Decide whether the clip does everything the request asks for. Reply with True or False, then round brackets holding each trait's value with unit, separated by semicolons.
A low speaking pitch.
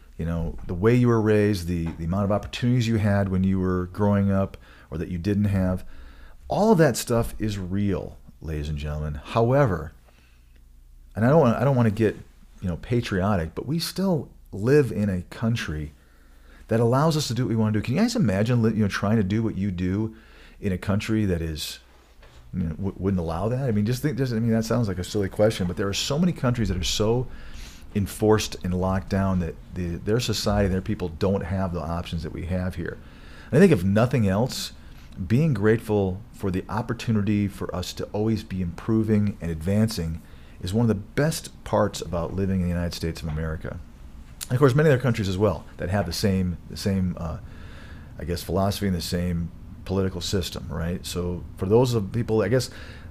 True (95 Hz)